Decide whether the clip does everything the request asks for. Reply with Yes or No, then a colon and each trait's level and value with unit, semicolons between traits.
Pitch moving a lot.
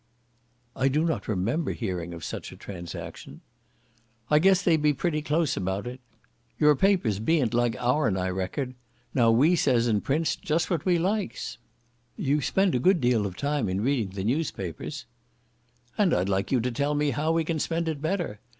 Yes: wide, 7.0 semitones